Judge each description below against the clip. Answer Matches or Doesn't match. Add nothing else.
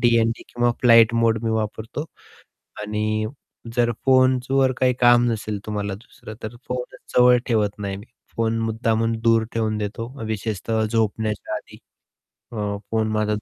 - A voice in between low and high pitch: Doesn't match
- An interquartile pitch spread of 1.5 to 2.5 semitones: Matches